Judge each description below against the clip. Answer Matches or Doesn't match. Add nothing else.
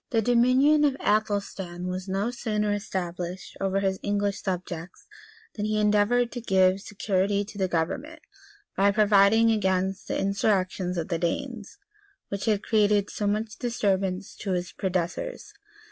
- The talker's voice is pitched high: Matches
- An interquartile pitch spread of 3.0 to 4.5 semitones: Doesn't match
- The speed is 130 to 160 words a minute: Matches